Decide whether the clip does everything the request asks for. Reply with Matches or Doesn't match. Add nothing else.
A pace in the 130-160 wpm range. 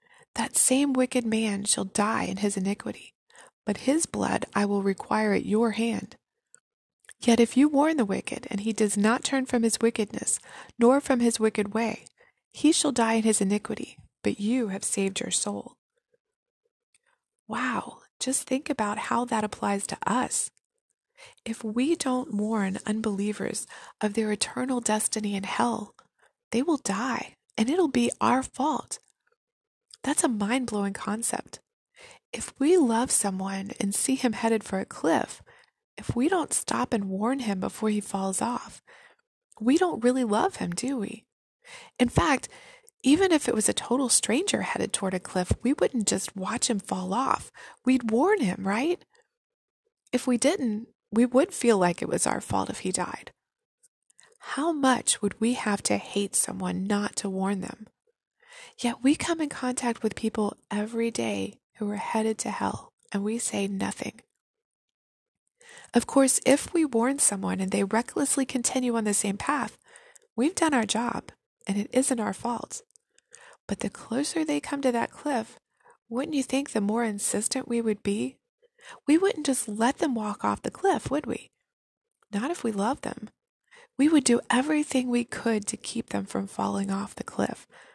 Doesn't match